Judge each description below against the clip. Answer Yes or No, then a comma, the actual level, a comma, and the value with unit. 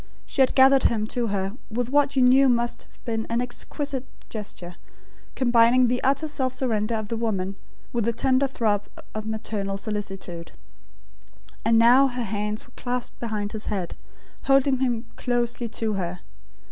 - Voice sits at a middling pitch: No, high, 235 Hz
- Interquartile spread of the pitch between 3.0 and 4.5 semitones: Yes, average, 3.4 semitones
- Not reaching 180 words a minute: Yes, average, 160 wpm